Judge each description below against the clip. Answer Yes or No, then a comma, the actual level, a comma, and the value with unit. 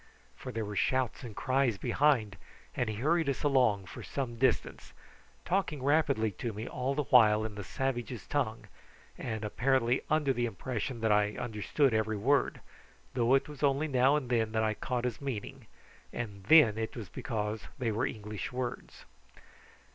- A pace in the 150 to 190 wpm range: Yes, average, 170 wpm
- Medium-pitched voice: No, low, 120 Hz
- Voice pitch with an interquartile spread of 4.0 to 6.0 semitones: No, average, 3.6 semitones